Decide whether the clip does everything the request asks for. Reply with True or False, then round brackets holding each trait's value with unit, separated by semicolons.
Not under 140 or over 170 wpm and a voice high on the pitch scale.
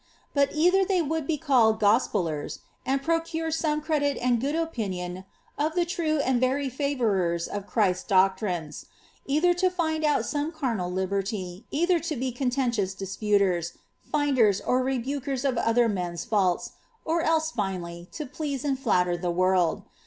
True (155 wpm; 255 Hz)